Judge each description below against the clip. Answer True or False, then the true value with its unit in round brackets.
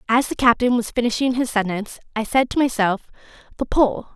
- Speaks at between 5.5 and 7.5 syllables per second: True (5.7 syllables/s)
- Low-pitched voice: False (235 Hz)